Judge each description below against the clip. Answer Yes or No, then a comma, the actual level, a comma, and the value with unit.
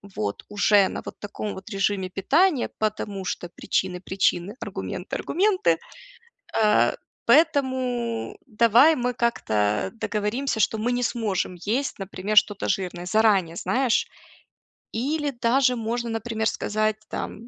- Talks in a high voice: Yes, high, 220 Hz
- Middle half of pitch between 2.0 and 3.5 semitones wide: No, average, 4.0 semitones